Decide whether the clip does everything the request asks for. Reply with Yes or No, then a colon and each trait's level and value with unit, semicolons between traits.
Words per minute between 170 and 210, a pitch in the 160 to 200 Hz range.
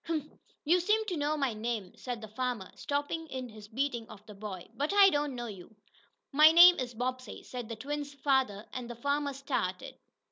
No: average, 200 wpm; very high, 255 Hz